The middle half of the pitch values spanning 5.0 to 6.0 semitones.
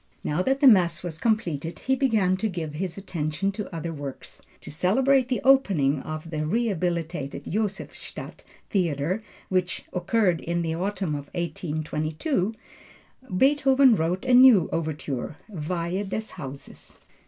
Yes: wide, 5.6 semitones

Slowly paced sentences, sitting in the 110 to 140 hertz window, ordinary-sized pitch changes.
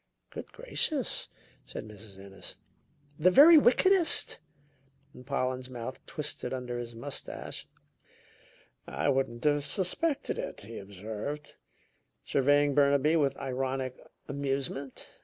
Yes: slow, 100 wpm; low, 135 Hz; average, 3.4 semitones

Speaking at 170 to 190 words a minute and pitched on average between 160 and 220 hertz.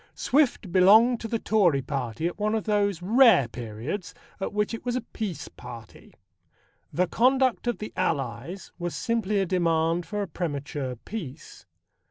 No: average, 160 wpm; medium, 185 Hz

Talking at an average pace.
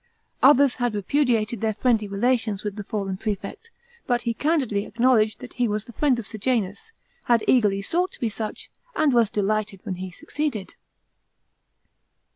Yes: average, 160 wpm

